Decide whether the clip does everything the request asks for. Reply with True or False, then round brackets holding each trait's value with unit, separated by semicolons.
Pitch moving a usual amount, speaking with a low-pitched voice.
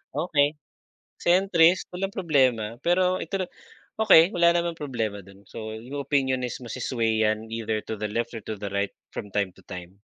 False (7.8 semitones; 120 Hz)